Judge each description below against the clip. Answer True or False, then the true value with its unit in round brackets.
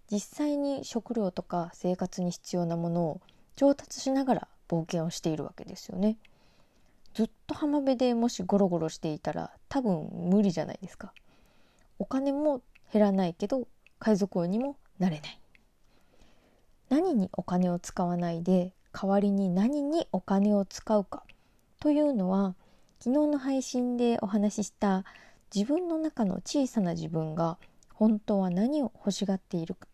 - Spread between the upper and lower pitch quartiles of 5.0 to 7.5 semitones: True (5.5 semitones)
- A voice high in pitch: True (200 Hz)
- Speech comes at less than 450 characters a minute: True (285 characters per minute)